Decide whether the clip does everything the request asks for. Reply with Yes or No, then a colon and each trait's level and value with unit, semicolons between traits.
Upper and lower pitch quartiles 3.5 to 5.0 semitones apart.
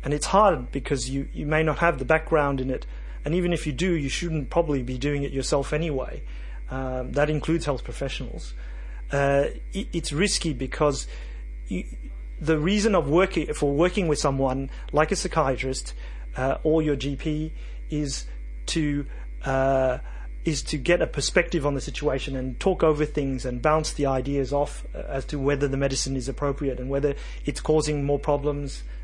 No: average, 2.9 semitones